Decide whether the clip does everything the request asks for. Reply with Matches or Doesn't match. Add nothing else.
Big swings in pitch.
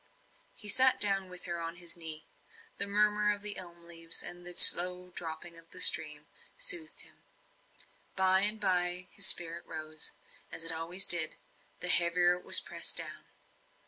Doesn't match